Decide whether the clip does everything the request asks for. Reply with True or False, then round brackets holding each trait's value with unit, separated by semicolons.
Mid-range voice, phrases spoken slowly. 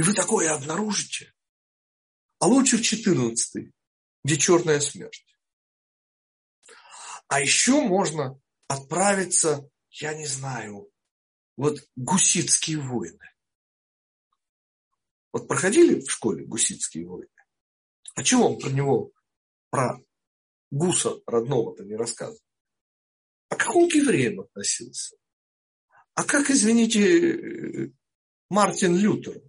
True (180 Hz; 100 wpm)